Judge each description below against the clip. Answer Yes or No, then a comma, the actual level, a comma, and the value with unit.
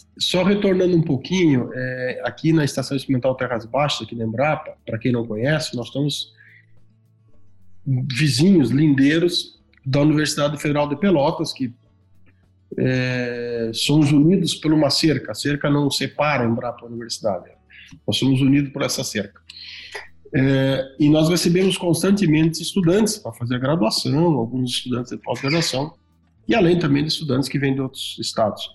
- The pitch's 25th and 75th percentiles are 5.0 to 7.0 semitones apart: No, average, 4.5 semitones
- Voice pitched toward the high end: No, low, 135 Hz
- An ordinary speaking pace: Yes, average, 150 wpm